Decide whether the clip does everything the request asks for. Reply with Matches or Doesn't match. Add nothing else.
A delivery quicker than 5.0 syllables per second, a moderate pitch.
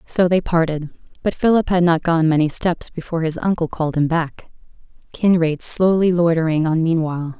Matches